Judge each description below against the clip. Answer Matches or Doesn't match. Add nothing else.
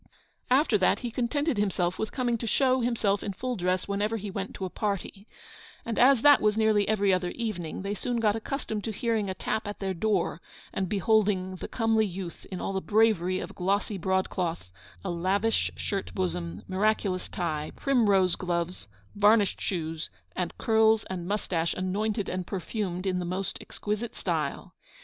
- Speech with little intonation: Doesn't match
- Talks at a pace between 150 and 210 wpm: Matches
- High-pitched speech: Matches